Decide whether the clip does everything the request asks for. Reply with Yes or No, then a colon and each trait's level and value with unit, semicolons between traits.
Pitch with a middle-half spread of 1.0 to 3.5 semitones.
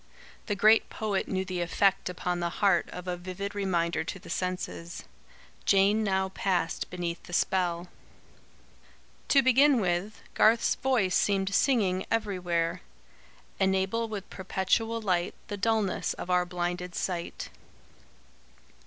Yes: narrow, 2.6 semitones